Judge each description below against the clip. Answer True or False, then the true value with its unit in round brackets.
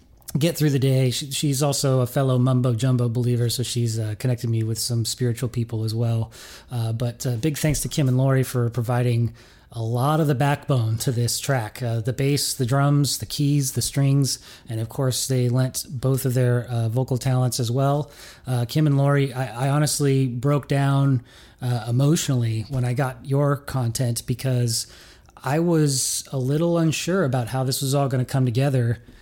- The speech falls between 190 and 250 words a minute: True (195 wpm)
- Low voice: True (130 Hz)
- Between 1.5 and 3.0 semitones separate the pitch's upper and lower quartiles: True (2.6 semitones)